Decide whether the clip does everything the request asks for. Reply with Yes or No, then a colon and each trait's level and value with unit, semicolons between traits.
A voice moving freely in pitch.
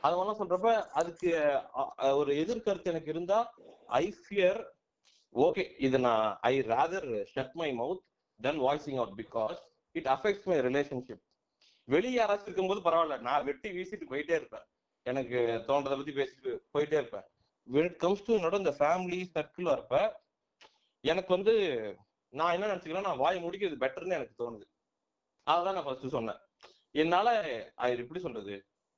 Yes: wide, 7.0 semitones